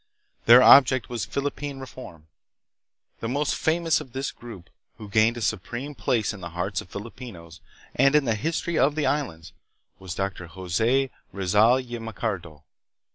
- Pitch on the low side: Yes, low, 115 Hz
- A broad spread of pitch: Yes, wide, 6.0 semitones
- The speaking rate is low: No, average, 155 wpm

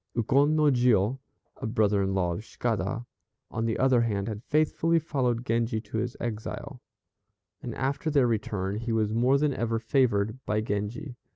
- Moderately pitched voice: No, low, 115 Hz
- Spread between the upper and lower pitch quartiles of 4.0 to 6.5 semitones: No, average, 3.6 semitones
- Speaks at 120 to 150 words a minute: No, average, 170 wpm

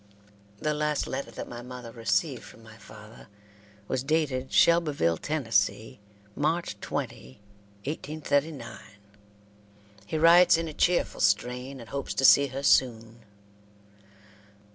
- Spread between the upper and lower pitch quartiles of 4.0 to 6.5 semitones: Yes, average, 5.1 semitones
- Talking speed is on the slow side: Yes, slow, 120 wpm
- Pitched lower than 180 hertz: Yes, low, 135 Hz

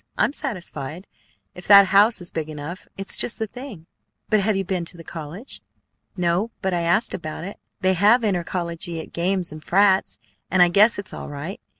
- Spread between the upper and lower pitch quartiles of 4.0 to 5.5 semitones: No, average, 3.1 semitones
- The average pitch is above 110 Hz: Yes, medium, 185 Hz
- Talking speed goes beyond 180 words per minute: Yes, average, 190 wpm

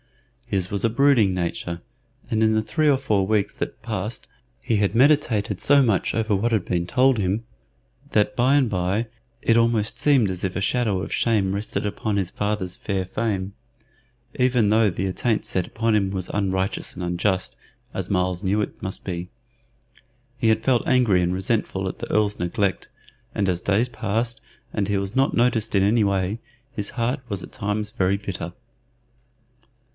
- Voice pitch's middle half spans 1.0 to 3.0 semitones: No, average, 3.4 semitones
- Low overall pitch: Yes, low, 105 Hz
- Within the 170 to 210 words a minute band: Yes, average, 180 wpm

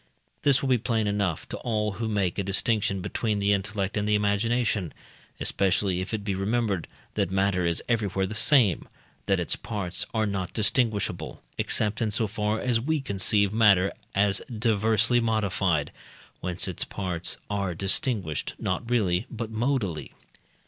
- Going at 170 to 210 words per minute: No, average, 155 wpm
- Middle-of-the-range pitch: No, low, 105 Hz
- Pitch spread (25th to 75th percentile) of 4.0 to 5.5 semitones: No, average, 2.7 semitones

